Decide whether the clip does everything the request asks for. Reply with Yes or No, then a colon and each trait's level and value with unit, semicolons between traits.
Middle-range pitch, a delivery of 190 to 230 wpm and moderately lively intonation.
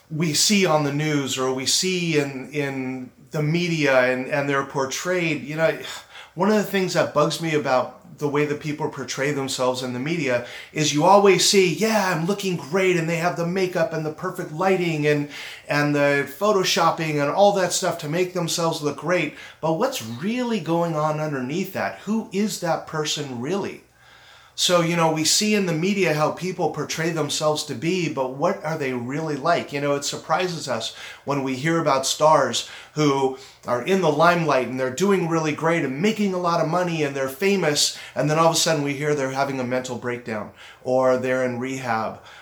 Yes: medium, 155 Hz; average, 200 wpm; average, 4.2 semitones